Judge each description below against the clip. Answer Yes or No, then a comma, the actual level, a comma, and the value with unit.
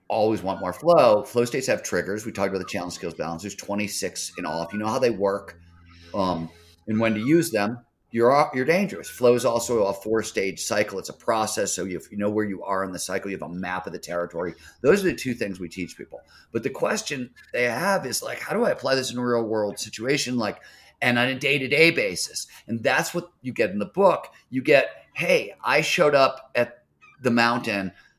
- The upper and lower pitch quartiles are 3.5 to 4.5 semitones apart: Yes, average, 4.1 semitones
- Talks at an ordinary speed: No, fast, 230 wpm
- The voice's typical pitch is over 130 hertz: No, low, 110 Hz